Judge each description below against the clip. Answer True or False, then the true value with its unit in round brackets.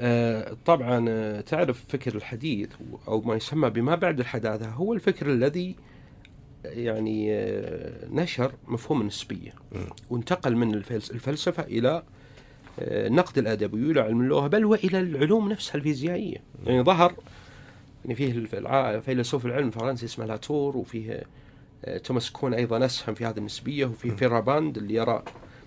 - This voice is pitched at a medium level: False (125 Hz)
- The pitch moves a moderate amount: True (4.3 semitones)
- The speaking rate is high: False (120 wpm)